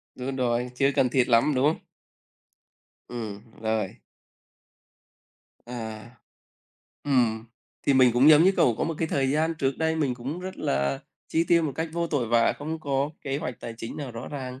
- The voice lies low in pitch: Yes, low, 130 Hz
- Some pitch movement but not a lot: Yes, average, 4.4 semitones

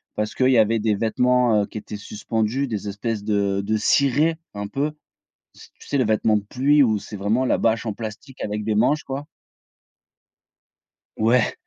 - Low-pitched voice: Yes, low, 110 Hz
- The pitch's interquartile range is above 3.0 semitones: Yes, average, 3.4 semitones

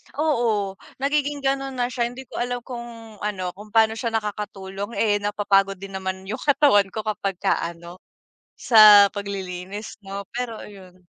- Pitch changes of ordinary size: Yes, average, 3.5 semitones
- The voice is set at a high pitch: Yes, high, 210 Hz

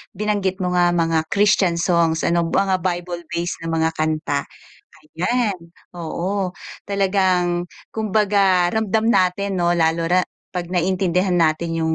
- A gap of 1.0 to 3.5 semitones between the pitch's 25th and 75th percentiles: Yes, narrow, 2.4 semitones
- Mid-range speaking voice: Yes, medium, 180 Hz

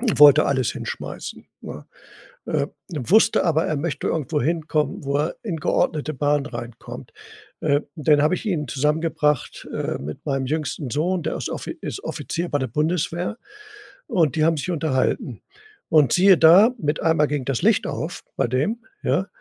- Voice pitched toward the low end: No, medium, 150 Hz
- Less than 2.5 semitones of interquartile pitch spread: No, average, 2.8 semitones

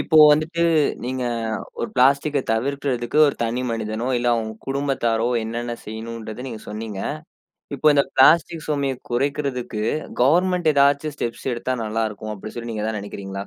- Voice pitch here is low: Yes, low, 125 Hz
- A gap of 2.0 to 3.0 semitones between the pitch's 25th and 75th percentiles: No, average, 4.0 semitones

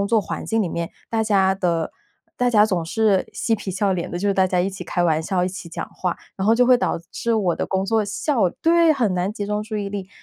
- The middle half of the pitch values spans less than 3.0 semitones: No, average, 3.4 semitones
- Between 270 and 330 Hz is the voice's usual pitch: No, high, 200 Hz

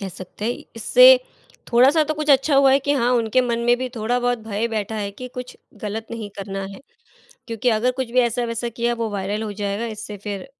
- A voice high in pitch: Yes, high, 230 Hz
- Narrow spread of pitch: No, average, 3.0 semitones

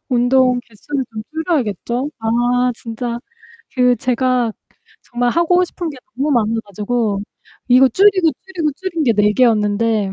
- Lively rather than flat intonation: No, average, 4.4 semitones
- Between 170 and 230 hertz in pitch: No, high, 245 Hz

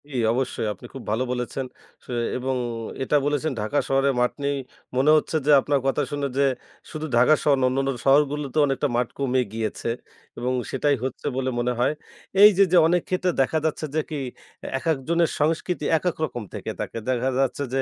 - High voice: No, medium, 140 Hz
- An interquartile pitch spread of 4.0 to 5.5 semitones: No, average, 3.0 semitones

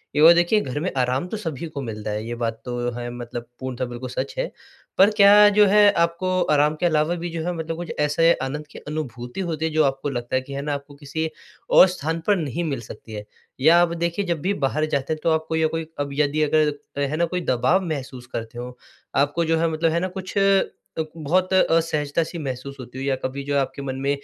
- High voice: No, medium, 150 Hz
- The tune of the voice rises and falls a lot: No, average, 4.2 semitones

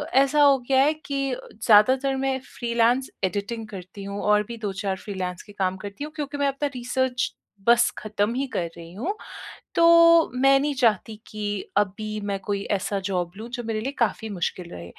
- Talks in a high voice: Yes, high, 220 Hz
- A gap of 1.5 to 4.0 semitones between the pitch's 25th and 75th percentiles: No, average, 5.1 semitones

